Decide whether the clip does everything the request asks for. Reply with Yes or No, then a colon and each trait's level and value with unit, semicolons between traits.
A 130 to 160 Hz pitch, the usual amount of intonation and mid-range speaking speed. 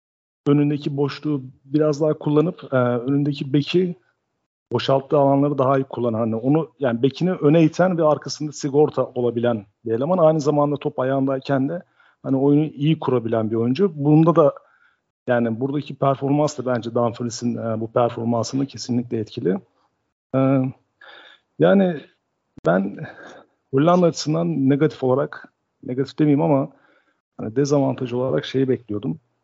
Yes: medium, 140 Hz; average, 3.3 semitones; average, 130 wpm